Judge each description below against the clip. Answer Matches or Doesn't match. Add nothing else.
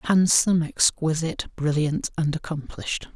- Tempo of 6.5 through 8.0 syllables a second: Doesn't match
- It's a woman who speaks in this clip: Doesn't match